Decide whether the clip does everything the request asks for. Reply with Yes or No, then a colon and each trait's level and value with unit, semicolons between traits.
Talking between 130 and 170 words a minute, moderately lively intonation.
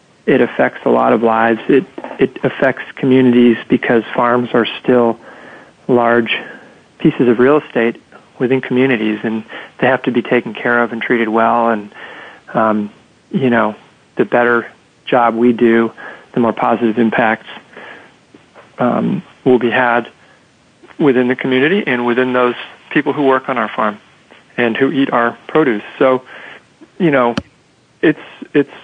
No: average, 150 wpm; narrow, 1.8 semitones